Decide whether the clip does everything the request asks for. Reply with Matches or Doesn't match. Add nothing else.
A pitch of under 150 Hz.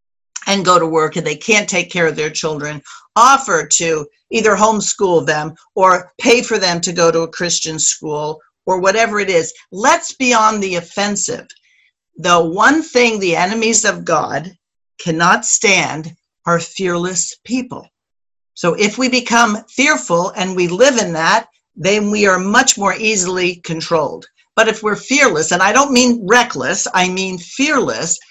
Doesn't match